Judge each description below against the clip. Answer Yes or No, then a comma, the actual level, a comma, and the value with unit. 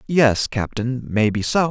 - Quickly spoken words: No, average, 140 wpm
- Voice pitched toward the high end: No, low, 125 Hz